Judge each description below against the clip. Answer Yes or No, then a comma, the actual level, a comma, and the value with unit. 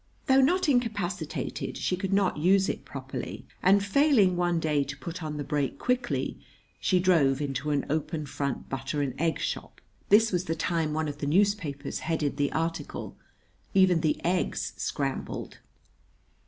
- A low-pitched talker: No, medium, 165 Hz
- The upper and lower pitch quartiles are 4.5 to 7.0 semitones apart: Yes, average, 4.8 semitones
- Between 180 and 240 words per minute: No, average, 160 wpm